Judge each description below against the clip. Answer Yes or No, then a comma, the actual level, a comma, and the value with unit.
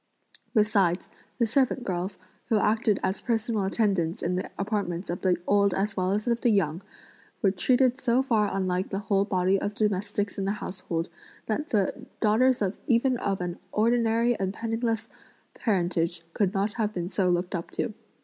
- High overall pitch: Yes, high, 205 Hz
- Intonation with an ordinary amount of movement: Yes, average, 3.4 semitones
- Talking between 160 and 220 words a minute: Yes, average, 170 wpm